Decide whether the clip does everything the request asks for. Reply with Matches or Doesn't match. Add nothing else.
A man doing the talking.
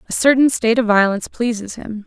Doesn't match